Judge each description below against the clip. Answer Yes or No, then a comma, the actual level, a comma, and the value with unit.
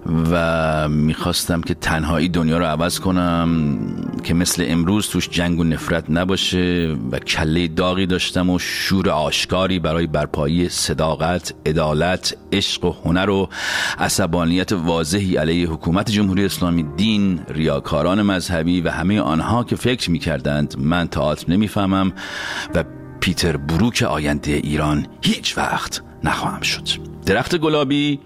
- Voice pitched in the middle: No, very low, 85 Hz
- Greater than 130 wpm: No, average, 125 wpm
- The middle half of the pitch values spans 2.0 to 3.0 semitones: Yes, average, 2.7 semitones